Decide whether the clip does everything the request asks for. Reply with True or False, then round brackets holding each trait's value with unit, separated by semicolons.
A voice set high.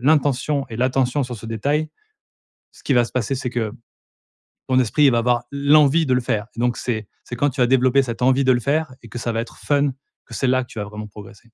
False (125 Hz)